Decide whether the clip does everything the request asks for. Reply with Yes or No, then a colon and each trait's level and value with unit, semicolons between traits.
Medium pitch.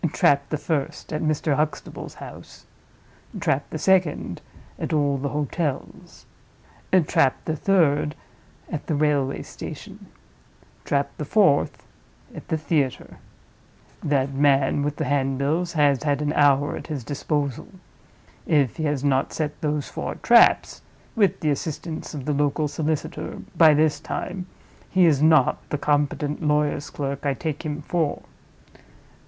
Yes: medium, 150 Hz